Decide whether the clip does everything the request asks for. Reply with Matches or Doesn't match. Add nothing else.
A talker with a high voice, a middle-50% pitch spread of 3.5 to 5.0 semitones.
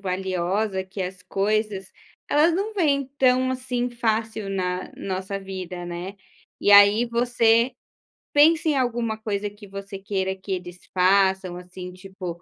Matches